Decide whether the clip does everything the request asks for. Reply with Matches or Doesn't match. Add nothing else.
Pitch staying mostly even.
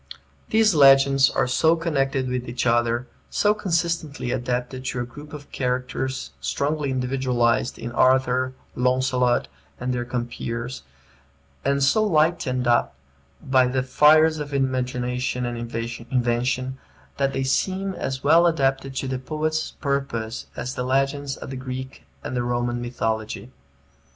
Matches